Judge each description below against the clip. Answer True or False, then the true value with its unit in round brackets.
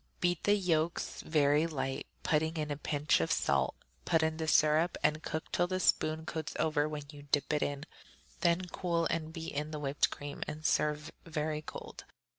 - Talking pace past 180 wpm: True (190 wpm)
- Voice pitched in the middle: True (155 Hz)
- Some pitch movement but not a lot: False (1.6 semitones)